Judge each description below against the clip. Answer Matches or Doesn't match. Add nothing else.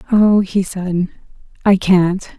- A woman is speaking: Matches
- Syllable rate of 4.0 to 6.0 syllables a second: Doesn't match